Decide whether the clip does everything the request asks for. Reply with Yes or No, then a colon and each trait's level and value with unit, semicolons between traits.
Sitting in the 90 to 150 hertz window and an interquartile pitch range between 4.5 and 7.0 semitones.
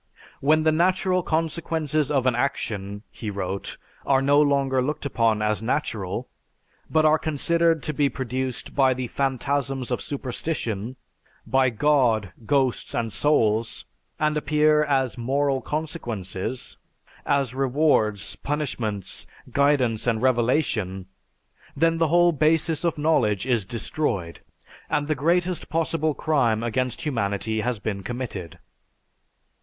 Yes: low, 135 Hz; average, 5.0 semitones